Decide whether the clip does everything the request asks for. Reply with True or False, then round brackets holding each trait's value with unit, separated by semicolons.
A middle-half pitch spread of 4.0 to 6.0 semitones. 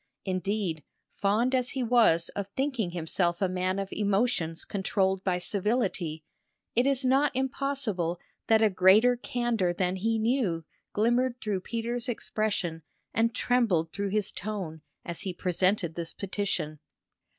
True (4.8 semitones)